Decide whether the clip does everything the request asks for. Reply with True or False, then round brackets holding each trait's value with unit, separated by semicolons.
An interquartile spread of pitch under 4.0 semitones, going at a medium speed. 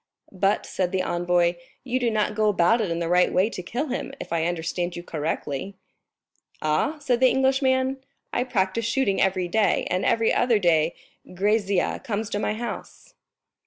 False (5.2 semitones; 175 wpm)